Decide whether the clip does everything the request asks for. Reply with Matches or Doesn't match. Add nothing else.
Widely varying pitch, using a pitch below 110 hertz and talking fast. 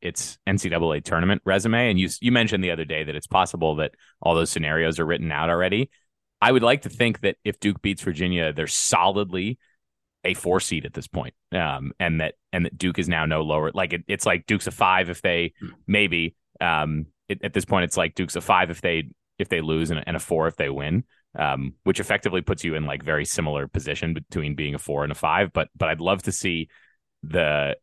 Doesn't match